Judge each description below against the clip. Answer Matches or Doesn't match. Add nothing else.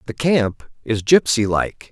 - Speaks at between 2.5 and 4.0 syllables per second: Matches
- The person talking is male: Matches